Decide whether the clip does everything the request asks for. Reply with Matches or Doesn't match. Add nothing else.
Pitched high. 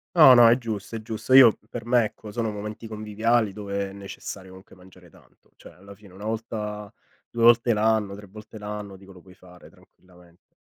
Doesn't match